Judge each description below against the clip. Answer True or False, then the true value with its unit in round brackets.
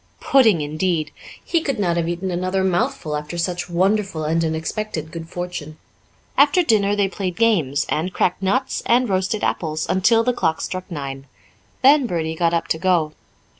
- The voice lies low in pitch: False (180 Hz)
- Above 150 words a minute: True (170 wpm)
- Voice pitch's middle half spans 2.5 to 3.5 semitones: False (4.3 semitones)